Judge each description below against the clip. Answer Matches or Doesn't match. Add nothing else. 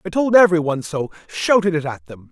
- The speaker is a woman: Doesn't match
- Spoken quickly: Matches